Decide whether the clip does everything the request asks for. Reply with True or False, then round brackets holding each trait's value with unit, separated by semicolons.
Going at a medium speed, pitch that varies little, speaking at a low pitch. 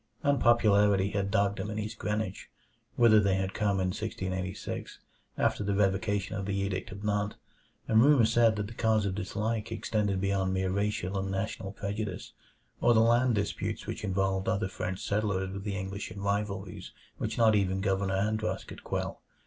True (175 wpm; 1.9 semitones; 100 Hz)